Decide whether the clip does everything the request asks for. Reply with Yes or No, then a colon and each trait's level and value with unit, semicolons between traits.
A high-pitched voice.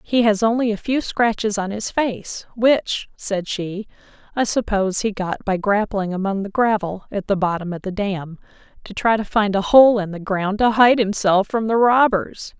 Yes: high, 205 Hz